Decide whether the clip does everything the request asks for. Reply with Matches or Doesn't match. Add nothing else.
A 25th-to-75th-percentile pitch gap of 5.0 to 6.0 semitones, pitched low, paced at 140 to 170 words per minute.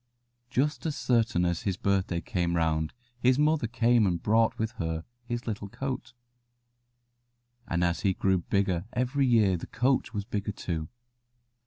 Matches